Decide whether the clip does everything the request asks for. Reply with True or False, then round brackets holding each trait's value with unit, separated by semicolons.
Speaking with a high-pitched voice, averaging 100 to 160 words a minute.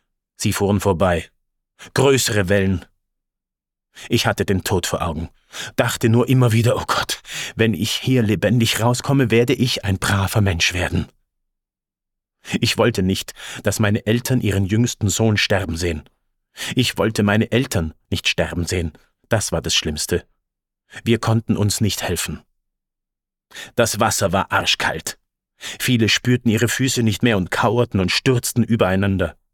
False (105 Hz; 140 wpm)